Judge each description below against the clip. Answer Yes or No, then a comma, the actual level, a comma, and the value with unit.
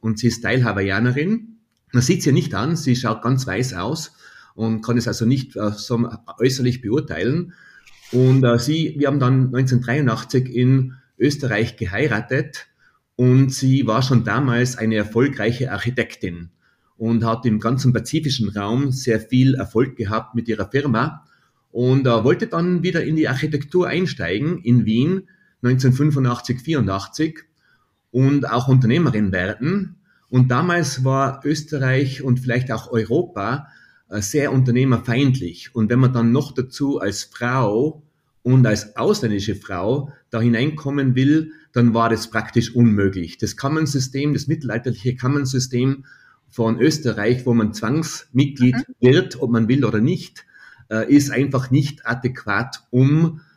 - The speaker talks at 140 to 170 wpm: No, average, 130 wpm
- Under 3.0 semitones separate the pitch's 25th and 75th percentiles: No, average, 3.3 semitones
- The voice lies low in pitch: Yes, low, 125 Hz